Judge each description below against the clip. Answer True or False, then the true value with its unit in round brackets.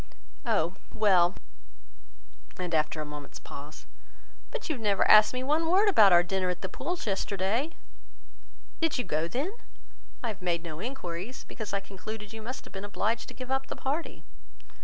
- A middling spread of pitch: False (6.4 semitones)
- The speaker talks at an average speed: True (180 wpm)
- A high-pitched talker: True (205 Hz)